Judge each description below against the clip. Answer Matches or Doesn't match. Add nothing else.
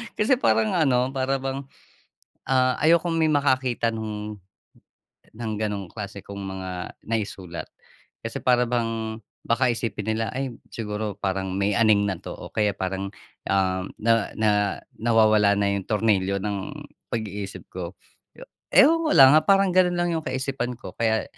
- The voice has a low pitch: Matches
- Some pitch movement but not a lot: Matches